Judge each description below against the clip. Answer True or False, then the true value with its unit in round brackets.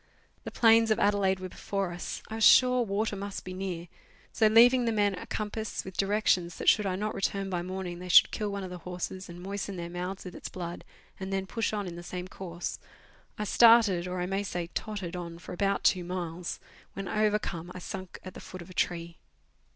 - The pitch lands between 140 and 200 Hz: True (190 Hz)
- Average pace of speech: False (220 wpm)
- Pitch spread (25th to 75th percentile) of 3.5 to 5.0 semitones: False (2.6 semitones)